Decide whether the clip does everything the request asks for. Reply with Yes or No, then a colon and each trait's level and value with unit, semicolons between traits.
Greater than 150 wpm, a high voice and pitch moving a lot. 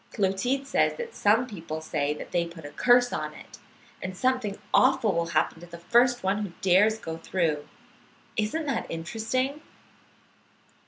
Yes: average, 165 wpm; high, 205 Hz; wide, 6.5 semitones